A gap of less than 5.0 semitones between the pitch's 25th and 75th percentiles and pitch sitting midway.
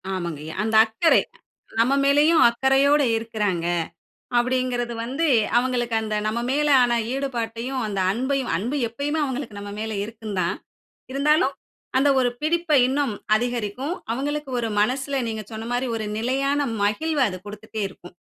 No: average, 4.2 semitones; high, 245 Hz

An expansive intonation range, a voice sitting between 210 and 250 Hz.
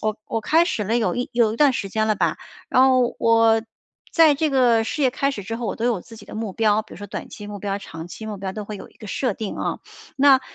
No: average, 3.4 semitones; high, 225 Hz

